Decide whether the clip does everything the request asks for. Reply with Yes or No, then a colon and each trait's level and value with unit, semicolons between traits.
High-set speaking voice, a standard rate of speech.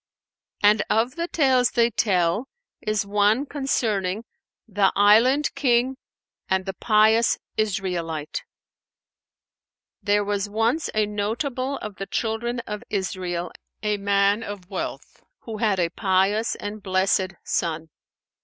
No: high, 210 Hz; slow, 125 wpm